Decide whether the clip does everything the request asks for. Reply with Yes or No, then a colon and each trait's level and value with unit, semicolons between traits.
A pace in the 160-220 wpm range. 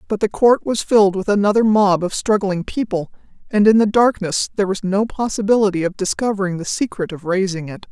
Yes: average, 195 wpm